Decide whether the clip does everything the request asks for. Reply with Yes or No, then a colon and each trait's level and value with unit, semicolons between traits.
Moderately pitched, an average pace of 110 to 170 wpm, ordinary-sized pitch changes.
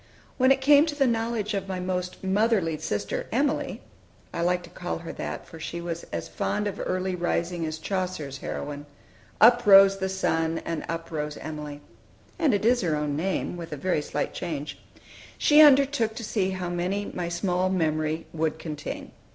No: medium, 180 Hz; average, 185 wpm; average, 4.4 semitones